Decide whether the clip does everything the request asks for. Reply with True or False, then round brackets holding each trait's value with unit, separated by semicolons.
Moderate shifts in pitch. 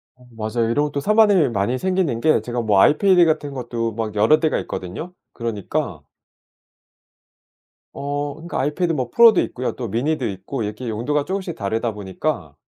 False (5.8 semitones)